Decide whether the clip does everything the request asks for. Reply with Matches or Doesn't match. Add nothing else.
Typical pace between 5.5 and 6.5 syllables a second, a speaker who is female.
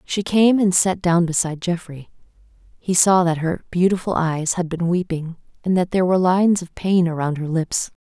Doesn't match